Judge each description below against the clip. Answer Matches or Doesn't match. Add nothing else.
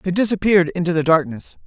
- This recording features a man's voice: Matches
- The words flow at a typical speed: Matches